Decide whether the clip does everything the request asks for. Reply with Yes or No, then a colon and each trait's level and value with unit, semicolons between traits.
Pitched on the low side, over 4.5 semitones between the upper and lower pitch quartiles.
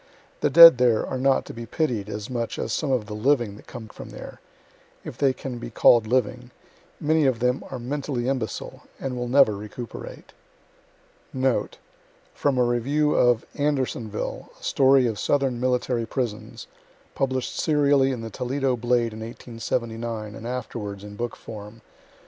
No: low, 125 Hz; average, 2.9 semitones